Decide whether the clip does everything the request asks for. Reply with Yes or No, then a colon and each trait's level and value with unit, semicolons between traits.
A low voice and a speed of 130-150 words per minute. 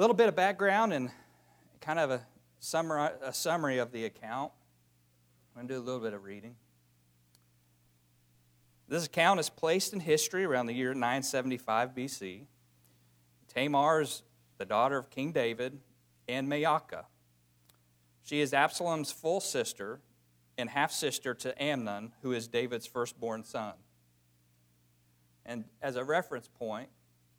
Yes: low, 115 Hz; average, 140 wpm